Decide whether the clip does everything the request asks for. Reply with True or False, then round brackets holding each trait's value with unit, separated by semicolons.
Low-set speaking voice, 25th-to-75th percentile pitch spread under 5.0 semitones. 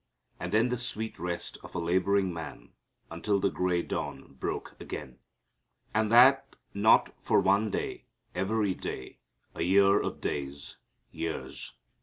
True (95 Hz; 3.9 semitones)